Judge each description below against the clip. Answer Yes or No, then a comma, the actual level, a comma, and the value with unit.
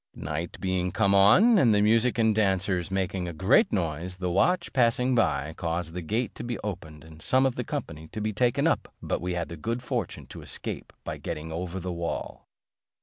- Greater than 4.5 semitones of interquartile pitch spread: Yes, average, 5.3 semitones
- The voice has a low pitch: Yes, very low, 95 Hz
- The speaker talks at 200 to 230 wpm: Yes, fast, 205 wpm